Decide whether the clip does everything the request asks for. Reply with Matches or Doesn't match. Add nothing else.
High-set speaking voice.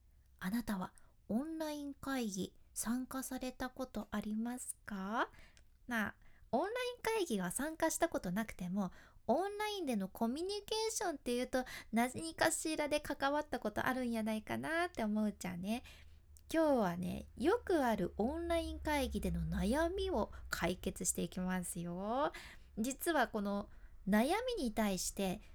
Matches